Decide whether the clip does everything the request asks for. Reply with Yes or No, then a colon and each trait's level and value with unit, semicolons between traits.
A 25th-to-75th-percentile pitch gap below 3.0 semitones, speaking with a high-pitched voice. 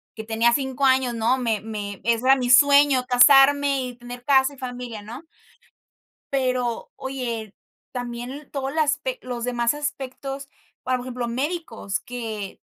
Yes: narrow, 2.4 semitones; very high, 250 Hz